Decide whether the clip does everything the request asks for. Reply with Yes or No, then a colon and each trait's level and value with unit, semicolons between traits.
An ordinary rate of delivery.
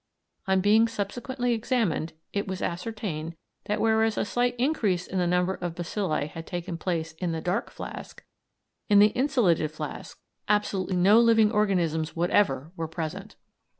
Yes: average, 150 wpm